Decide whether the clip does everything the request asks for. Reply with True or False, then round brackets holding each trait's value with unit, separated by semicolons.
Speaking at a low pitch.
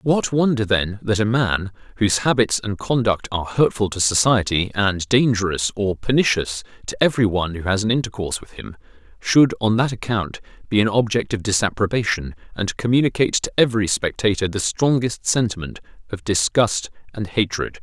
True (105 Hz)